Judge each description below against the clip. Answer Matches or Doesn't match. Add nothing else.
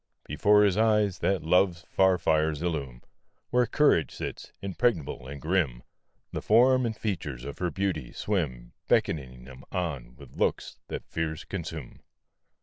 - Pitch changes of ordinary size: Doesn't match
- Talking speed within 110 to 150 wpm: Matches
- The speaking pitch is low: Matches